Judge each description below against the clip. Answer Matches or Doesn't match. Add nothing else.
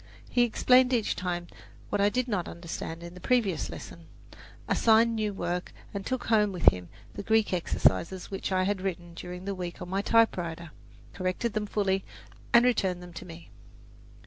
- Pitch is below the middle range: Doesn't match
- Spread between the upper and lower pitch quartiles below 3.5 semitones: Doesn't match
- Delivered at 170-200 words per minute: Matches